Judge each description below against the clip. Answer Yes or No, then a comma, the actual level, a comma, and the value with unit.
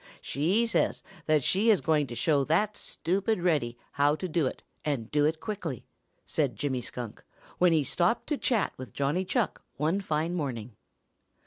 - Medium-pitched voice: Yes, medium, 155 Hz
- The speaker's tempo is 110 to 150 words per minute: No, average, 175 wpm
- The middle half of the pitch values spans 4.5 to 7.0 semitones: Yes, average, 5.1 semitones